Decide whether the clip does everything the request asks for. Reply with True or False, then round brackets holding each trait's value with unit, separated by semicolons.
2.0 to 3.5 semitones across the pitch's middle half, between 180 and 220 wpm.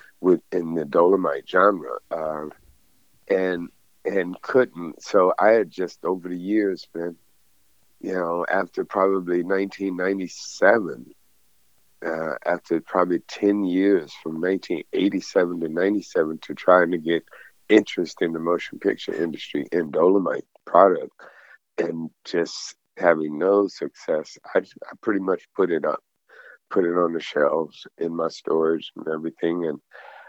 False (2.4 semitones; 135 wpm)